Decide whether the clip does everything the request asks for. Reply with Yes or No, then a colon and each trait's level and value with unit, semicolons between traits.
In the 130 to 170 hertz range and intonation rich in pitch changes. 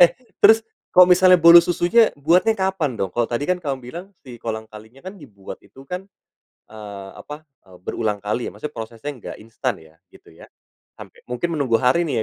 Yes: low, 135 Hz; wide, 7.5 semitones